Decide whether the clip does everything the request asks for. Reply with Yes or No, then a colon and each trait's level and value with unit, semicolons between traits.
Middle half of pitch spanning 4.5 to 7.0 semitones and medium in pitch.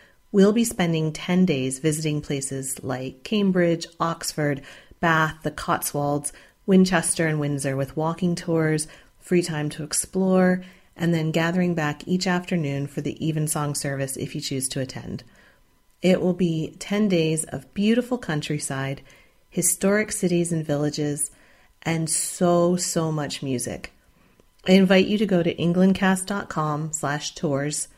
No: average, 3.7 semitones; medium, 160 Hz